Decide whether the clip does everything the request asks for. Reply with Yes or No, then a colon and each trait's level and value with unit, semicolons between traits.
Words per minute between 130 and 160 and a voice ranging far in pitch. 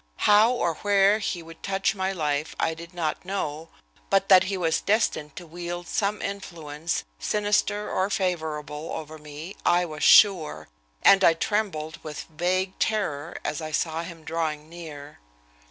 No: average, 155 wpm; average, 3.9 semitones